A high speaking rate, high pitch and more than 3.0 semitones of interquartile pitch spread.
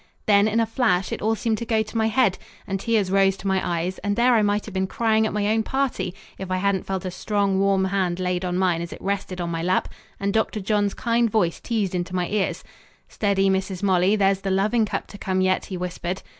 No: fast, 245 wpm; high, 195 Hz; narrow, 2.5 semitones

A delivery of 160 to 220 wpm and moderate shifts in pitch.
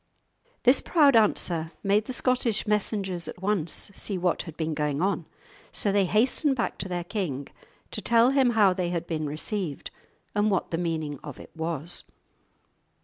Yes: average, 170 wpm; average, 4.7 semitones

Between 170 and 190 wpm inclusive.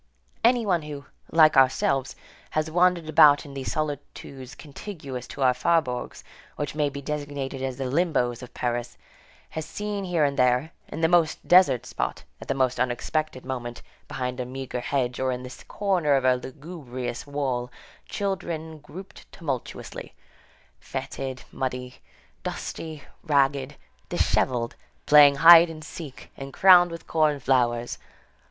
No: average, 145 wpm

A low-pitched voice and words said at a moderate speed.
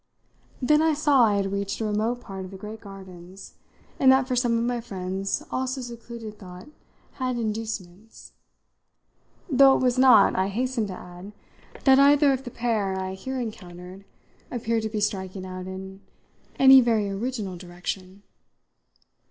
No: high, 215 Hz; average, 160 wpm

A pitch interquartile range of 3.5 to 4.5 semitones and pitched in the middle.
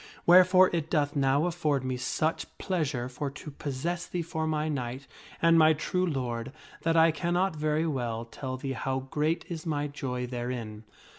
Yes: average, 4.1 semitones; medium, 150 Hz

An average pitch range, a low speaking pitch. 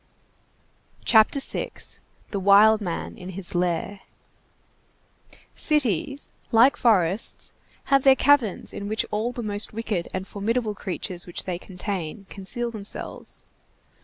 No: average, 3.8 semitones; high, 205 Hz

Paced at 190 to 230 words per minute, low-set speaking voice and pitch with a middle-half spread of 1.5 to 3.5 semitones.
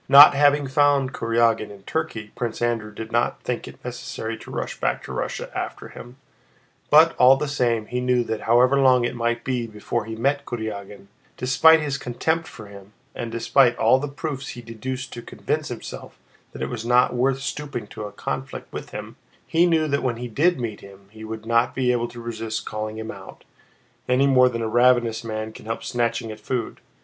Yes: average, 200 wpm; low, 120 Hz; average, 3.1 semitones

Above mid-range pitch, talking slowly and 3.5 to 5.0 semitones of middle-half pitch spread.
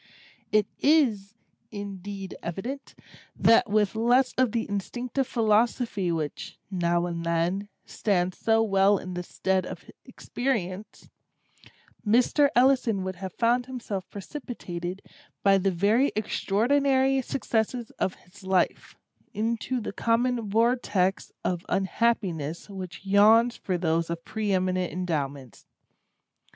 Yes: high, 205 Hz; slow, 115 wpm; average, 4.2 semitones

